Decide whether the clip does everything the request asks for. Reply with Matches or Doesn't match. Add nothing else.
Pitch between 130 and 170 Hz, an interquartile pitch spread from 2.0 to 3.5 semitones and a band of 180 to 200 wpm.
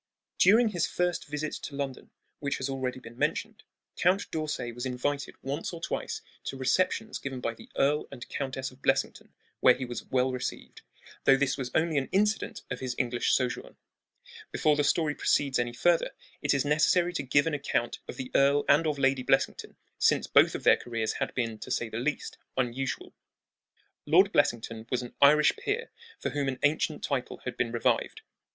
Matches